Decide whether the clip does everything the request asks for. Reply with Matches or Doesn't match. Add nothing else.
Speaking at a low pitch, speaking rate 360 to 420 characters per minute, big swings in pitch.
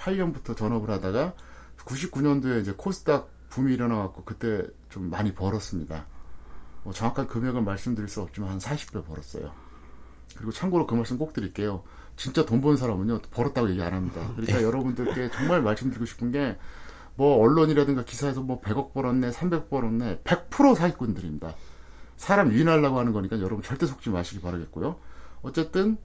Matches